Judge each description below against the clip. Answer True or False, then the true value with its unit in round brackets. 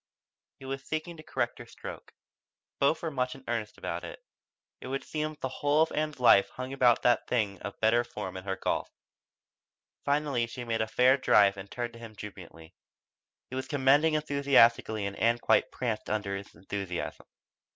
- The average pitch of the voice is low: True (120 Hz)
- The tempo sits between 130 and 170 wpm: False (185 wpm)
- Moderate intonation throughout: True (4.9 semitones)